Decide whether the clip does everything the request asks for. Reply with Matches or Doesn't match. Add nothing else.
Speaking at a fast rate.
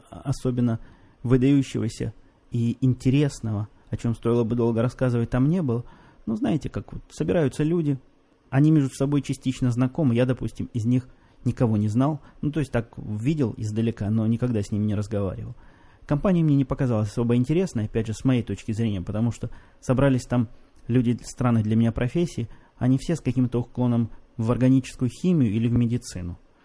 Matches